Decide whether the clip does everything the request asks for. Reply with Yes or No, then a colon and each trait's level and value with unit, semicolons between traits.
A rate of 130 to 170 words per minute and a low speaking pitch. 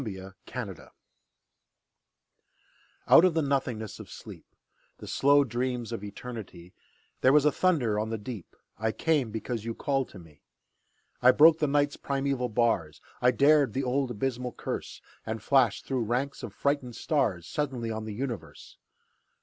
Yes: average, 155 wpm; low, 125 Hz